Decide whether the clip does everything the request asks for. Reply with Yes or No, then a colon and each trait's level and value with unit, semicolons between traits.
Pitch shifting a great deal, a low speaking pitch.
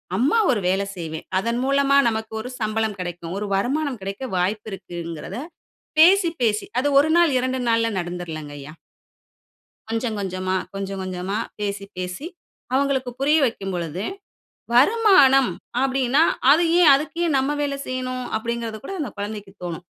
No: wide, 6.1 semitones; high, 225 Hz